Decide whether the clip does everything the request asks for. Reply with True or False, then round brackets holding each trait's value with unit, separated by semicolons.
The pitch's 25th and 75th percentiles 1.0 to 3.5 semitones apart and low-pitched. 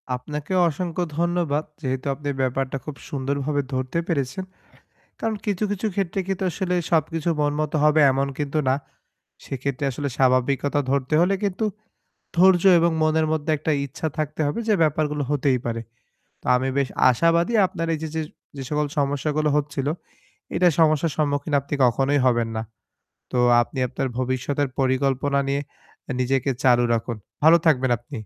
False (3.2 semitones; 145 Hz)